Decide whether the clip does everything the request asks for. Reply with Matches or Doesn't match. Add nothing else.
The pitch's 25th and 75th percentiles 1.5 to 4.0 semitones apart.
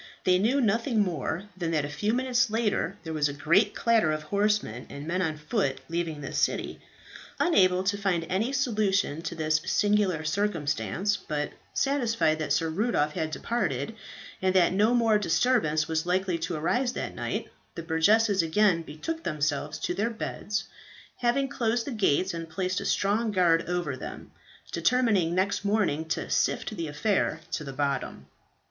Doesn't match